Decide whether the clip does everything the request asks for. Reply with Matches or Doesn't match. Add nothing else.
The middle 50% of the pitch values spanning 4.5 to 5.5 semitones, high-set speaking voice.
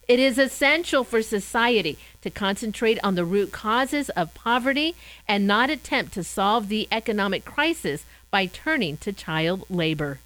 Matches